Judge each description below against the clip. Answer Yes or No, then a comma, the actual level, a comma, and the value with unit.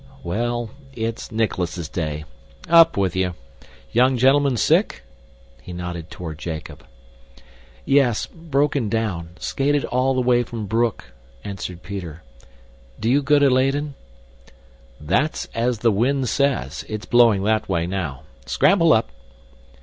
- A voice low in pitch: Yes, low, 115 Hz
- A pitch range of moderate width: No, wide, 6.8 semitones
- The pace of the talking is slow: Yes, slow, 125 wpm